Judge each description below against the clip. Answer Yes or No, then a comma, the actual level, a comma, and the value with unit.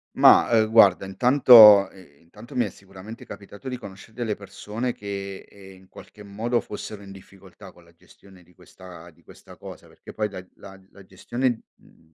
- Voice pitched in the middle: No, low, 100 Hz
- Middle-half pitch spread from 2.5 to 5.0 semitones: Yes, average, 2.8 semitones